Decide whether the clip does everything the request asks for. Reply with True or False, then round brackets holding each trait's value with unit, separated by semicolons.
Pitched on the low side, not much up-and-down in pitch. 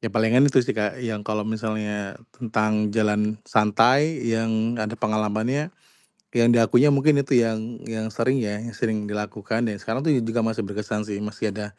True (110 Hz; 1.9 semitones)